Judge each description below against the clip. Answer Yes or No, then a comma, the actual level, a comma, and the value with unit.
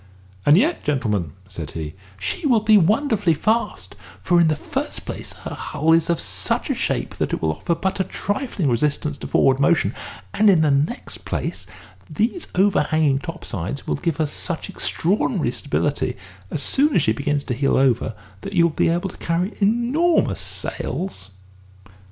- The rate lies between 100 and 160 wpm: No, average, 175 wpm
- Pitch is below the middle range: No, medium, 160 Hz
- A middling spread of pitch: No, wide, 6.4 semitones